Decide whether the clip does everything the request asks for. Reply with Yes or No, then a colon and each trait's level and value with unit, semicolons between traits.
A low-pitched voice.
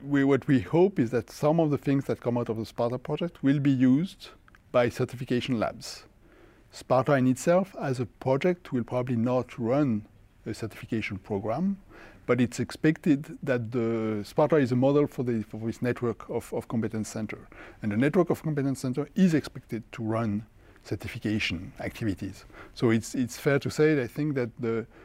Yes: low, 125 Hz